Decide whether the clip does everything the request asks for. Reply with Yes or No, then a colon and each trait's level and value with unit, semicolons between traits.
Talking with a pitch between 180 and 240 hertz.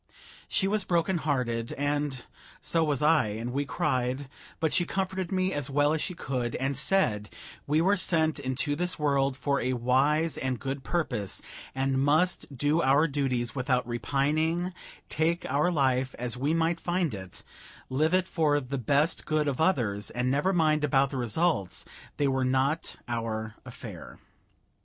No: medium, 145 Hz